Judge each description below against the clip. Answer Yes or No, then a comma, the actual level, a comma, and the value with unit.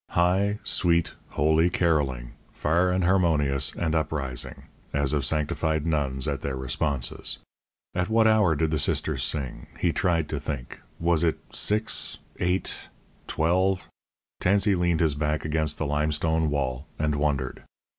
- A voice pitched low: Yes, very low, 80 Hz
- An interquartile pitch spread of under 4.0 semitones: Yes, average, 3.3 semitones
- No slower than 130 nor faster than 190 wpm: Yes, average, 140 wpm